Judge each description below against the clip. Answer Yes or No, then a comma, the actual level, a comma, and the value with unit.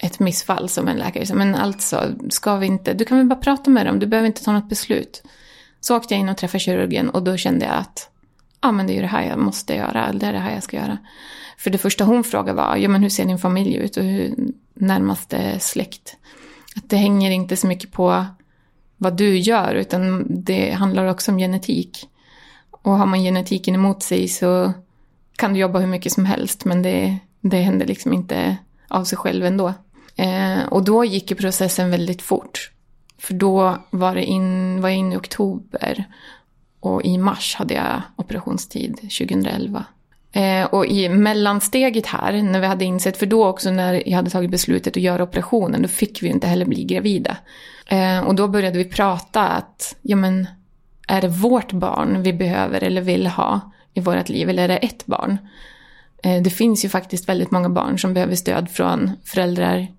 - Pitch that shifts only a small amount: Yes, narrow, 2.0 semitones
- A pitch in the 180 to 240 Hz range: Yes, high, 190 Hz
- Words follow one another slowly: No, average, 200 wpm